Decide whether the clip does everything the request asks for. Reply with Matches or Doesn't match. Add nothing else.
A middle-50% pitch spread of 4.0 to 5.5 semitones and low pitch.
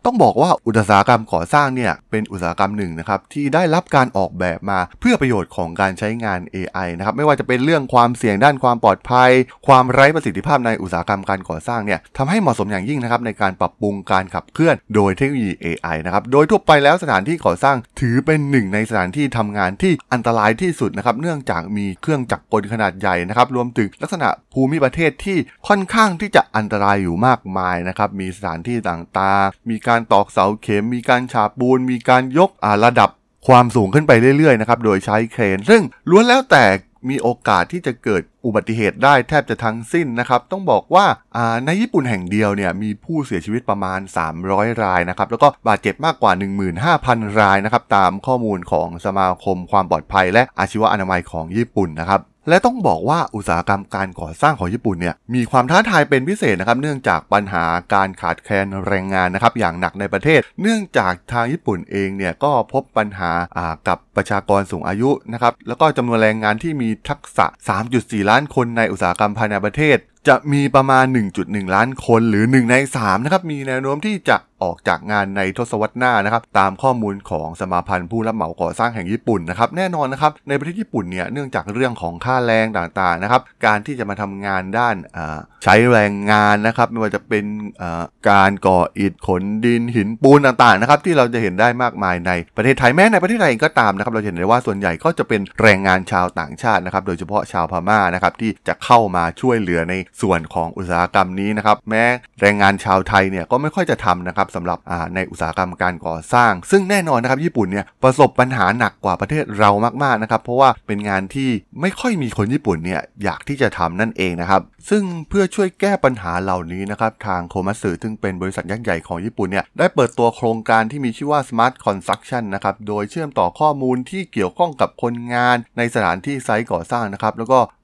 Matches